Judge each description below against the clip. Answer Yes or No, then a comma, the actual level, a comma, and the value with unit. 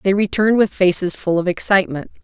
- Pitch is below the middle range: No, high, 190 Hz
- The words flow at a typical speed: Yes, average, 190 wpm